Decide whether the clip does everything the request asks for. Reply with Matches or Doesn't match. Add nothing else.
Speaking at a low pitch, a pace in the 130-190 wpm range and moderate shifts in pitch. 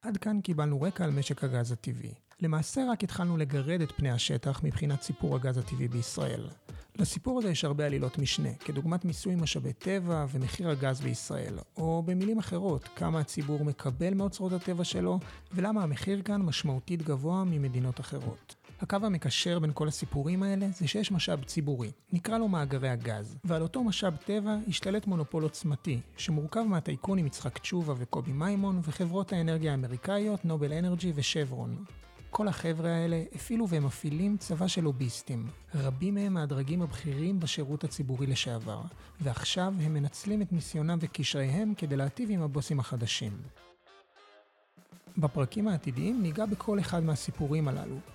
Doesn't match